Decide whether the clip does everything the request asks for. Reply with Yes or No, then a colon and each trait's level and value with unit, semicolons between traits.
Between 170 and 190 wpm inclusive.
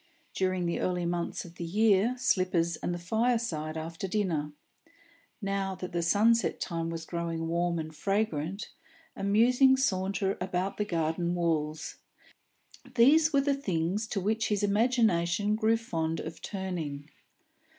No: average, 140 wpm